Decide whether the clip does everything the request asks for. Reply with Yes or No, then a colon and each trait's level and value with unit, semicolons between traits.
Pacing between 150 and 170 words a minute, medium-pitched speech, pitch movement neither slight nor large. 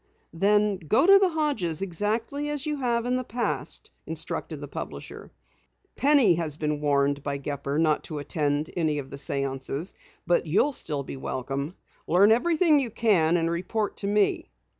No: average, 165 wpm; medium, 175 Hz; wide, 8.2 semitones